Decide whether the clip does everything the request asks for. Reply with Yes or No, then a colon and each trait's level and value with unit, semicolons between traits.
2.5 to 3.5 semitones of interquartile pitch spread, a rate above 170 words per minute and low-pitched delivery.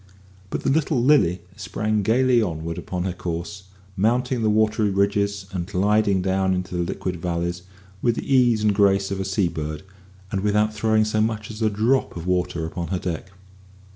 Yes: average, 3.1 semitones; average, 180 wpm; low, 100 Hz